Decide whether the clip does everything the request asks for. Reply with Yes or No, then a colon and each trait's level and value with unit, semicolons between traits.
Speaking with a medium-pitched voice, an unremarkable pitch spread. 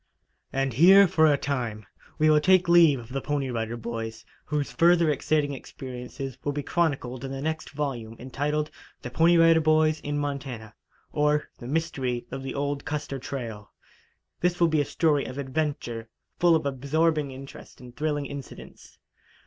Yes: medium, 145 Hz; average, 3.4 semitones